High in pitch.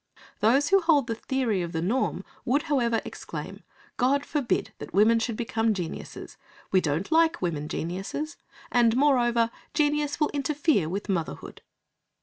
Yes: high, 235 Hz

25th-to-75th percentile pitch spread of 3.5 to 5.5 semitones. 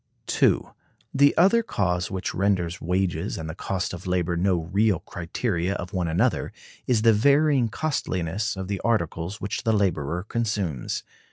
Yes: average, 4.3 semitones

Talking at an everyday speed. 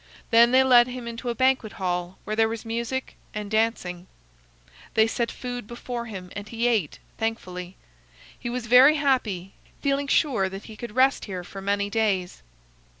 Yes: average, 170 wpm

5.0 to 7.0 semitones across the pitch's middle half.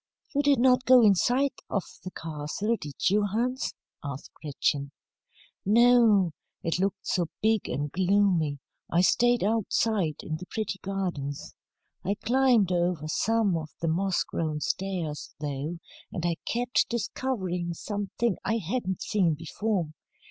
Yes: wide, 5.4 semitones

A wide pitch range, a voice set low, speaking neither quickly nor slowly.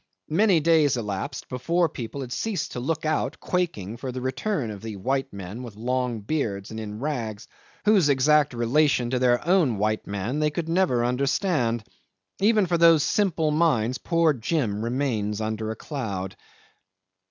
Yes: wide, 6.0 semitones; low, 130 Hz; average, 165 wpm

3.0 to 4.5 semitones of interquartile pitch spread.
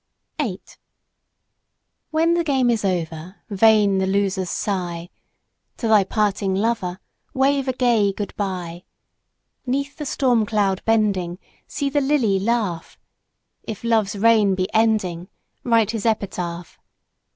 Yes: average, 3.8 semitones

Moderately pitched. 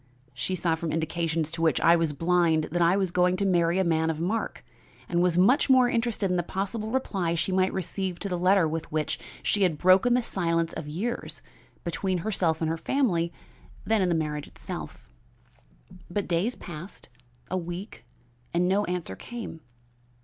Yes: medium, 175 Hz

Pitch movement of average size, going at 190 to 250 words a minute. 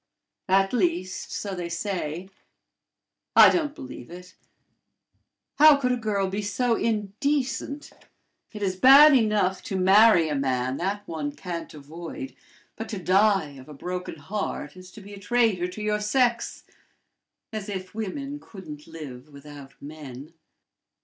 No: average, 5.0 semitones; average, 145 wpm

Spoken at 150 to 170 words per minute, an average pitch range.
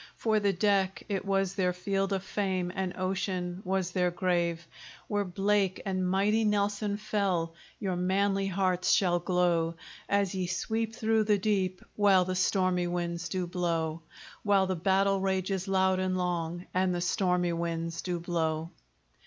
No: average, 155 wpm; narrow, 1.9 semitones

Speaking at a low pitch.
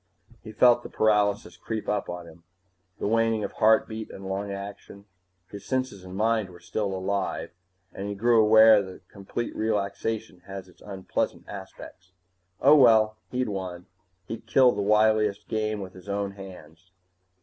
Yes: low, 100 Hz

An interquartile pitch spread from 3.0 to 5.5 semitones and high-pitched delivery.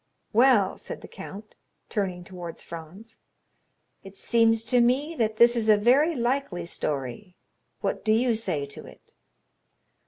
Yes: average, 4.7 semitones; high, 215 Hz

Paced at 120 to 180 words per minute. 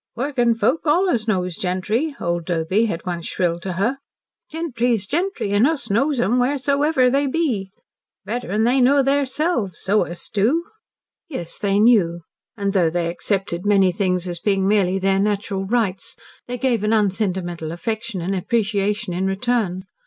Yes: average, 155 wpm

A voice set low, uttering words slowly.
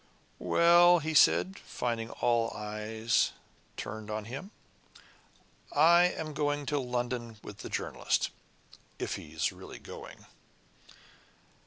Yes: low, 125 Hz; slow, 115 wpm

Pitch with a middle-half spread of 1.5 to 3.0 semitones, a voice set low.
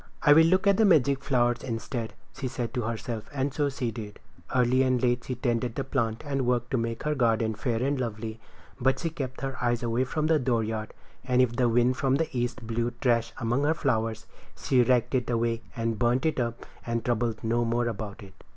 Yes: narrow, 2.6 semitones; low, 120 Hz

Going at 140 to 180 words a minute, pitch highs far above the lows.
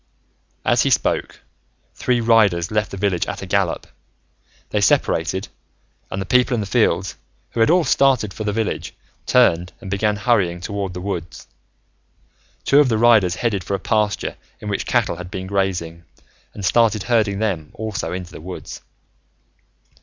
No: average, 165 wpm; average, 3.6 semitones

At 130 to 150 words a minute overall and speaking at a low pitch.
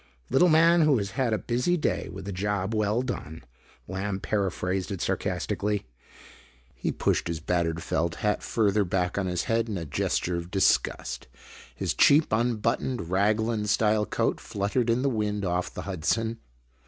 No: average, 165 wpm; low, 105 Hz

